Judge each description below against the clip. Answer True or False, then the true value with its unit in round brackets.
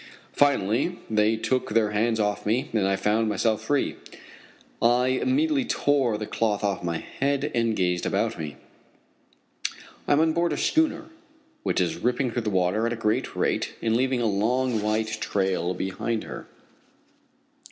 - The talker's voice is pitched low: True (115 Hz)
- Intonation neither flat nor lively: True (3.9 semitones)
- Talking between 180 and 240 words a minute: False (165 wpm)